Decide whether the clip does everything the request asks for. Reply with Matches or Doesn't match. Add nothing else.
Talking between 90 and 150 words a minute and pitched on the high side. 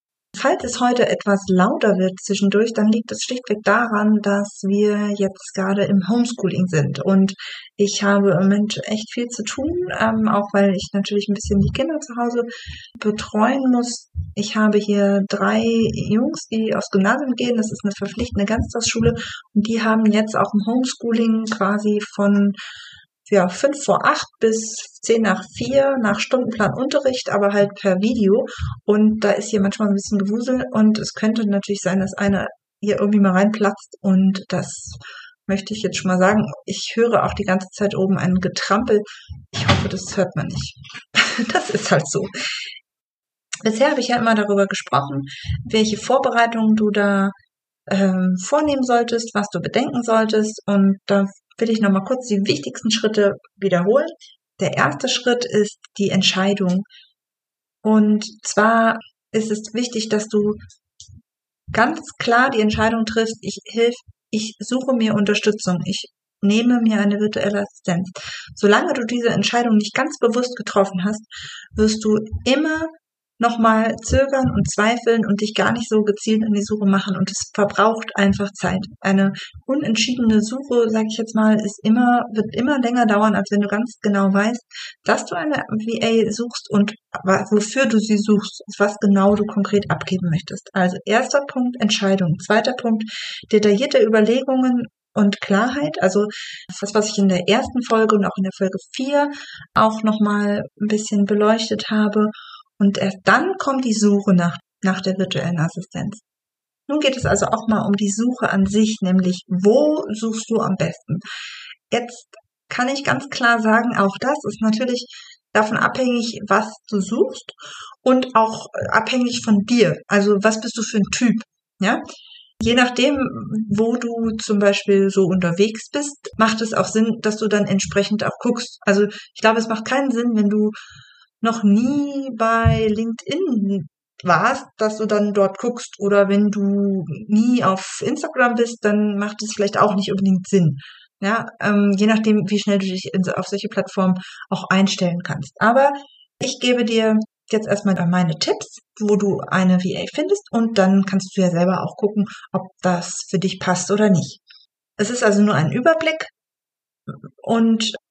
Doesn't match